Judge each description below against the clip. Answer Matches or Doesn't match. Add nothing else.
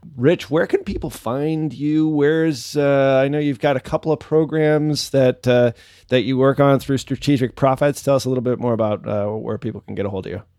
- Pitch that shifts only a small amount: Doesn't match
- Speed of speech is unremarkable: Doesn't match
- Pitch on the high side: Doesn't match